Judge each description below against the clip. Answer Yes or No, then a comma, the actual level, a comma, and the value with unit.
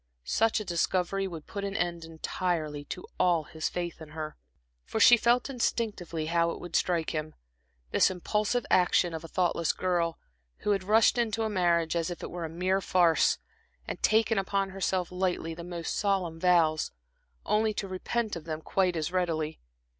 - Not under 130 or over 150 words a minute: No, average, 175 wpm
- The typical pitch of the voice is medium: Yes, medium, 180 Hz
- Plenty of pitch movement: No, average, 3.1 semitones